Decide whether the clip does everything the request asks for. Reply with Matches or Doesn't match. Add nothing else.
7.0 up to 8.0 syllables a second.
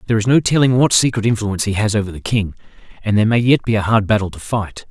Matches